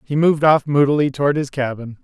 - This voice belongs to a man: Yes, male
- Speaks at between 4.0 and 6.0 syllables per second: No, 6.3 syllables/s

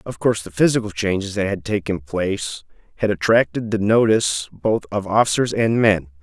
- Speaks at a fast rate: No, average, 175 wpm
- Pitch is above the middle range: No, low, 100 Hz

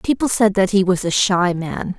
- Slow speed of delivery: No, fast, 240 wpm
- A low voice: No, high, 190 Hz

